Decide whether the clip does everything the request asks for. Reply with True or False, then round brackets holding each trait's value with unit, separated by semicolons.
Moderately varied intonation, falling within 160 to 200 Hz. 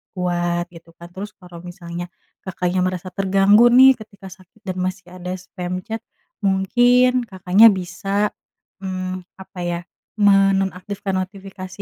False (1.8 semitones; 190 Hz)